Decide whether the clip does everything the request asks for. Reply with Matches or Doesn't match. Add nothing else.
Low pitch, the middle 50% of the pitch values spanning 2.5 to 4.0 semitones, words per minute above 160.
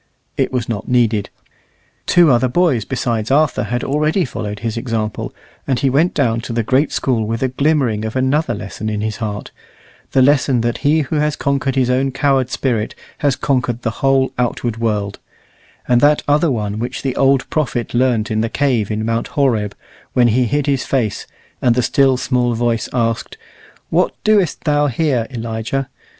Matches